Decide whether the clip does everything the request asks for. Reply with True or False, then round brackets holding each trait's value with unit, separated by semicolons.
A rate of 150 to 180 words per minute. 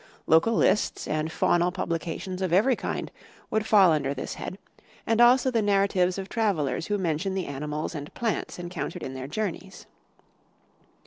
True (155 wpm)